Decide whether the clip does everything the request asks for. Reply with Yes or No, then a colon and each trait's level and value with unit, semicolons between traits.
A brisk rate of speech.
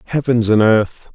No: average, 160 wpm